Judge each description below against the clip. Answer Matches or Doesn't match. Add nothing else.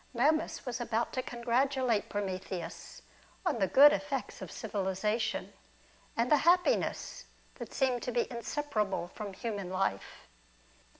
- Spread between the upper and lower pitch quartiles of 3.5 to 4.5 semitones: Doesn't match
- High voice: Matches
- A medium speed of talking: Doesn't match